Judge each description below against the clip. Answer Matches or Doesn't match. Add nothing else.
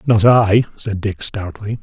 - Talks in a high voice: Doesn't match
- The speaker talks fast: Doesn't match